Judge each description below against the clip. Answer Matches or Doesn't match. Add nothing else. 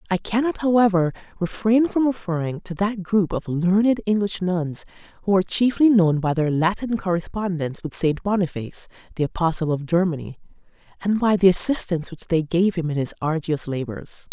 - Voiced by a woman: Matches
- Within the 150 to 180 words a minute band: Matches